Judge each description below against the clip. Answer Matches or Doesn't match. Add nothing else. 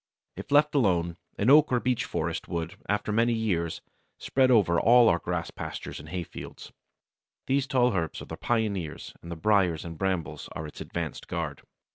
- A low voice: Matches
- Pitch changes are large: Matches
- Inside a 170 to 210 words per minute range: Matches